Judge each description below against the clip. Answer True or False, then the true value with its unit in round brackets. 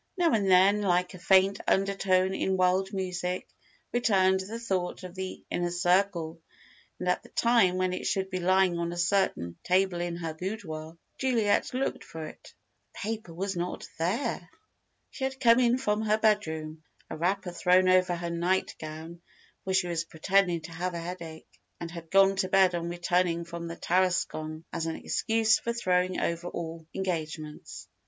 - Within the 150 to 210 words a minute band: True (175 wpm)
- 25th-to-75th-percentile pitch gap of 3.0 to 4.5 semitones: False (2.4 semitones)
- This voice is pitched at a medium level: True (180 Hz)